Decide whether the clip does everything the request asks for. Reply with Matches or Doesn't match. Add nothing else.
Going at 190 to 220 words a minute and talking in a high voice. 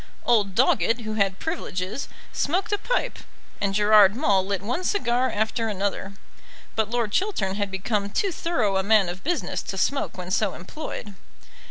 Doesn't match